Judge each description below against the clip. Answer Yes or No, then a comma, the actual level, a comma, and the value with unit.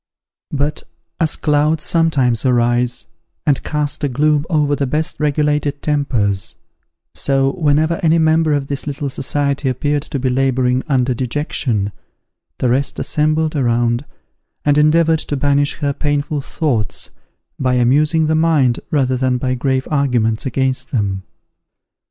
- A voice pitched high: No, medium, 140 Hz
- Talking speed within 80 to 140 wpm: Yes, slow, 135 wpm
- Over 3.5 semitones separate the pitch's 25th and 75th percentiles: No, average, 2.9 semitones